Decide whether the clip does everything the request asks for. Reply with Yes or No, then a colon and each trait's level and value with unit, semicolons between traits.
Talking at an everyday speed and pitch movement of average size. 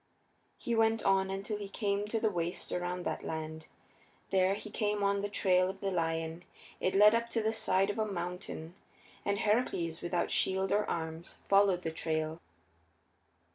Yes: average, 170 wpm; average, 3.1 semitones